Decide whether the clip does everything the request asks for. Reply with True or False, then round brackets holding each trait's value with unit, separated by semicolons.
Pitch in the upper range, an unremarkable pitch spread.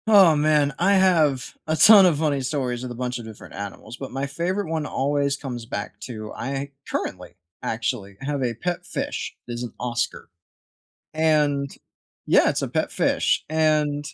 False (140 Hz; 4.3 semitones)